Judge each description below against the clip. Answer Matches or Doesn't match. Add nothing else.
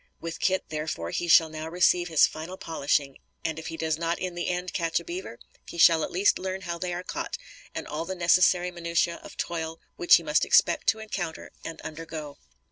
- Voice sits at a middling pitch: Matches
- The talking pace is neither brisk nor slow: Doesn't match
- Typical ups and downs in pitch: Doesn't match